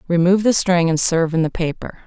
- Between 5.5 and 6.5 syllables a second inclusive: Yes, 6.4 syllables/s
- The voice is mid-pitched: Yes, medium, 175 Hz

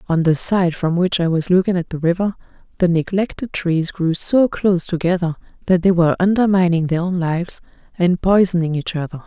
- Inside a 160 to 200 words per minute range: Yes, average, 190 wpm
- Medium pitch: Yes, medium, 175 Hz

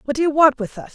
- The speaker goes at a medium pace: No, fast, 380 wpm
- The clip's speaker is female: Yes, female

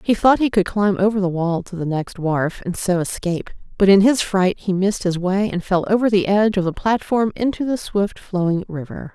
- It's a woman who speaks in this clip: Yes, female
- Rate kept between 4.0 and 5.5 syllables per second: Yes, 5.3 syllables/s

